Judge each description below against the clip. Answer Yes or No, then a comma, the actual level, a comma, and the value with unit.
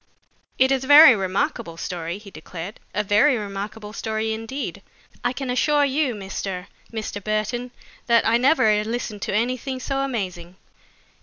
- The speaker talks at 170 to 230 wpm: No, average, 150 wpm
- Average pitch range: Yes, average, 4.4 semitones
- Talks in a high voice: Yes, high, 220 Hz